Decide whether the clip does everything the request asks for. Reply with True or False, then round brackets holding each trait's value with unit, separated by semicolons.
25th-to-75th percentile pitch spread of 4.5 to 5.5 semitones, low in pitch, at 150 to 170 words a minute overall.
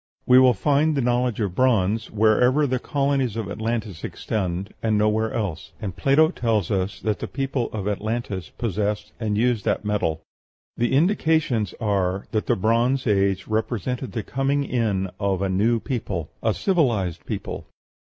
False (4.0 semitones; 110 Hz; 160 wpm)